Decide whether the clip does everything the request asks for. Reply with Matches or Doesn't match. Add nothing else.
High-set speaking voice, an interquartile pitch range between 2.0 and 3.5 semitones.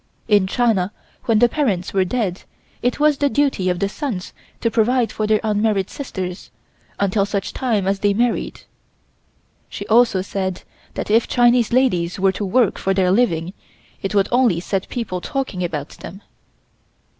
Doesn't match